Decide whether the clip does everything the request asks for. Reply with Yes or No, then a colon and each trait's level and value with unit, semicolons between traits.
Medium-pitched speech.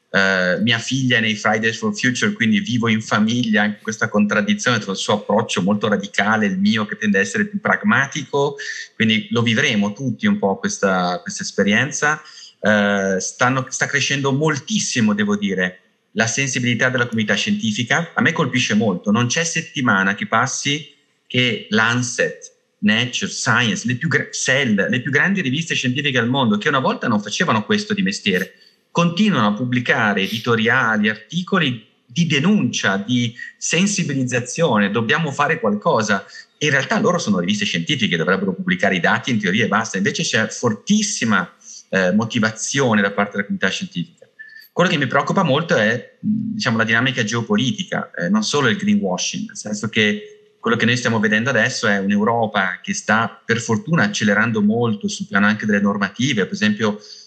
No: low, 125 Hz